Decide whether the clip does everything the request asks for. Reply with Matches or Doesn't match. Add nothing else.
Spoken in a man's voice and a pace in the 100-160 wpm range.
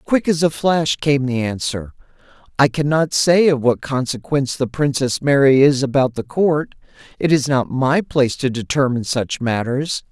Doesn't match